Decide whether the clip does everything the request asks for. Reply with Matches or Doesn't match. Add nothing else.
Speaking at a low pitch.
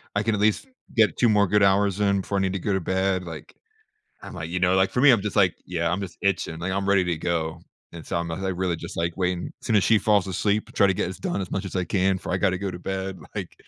Matches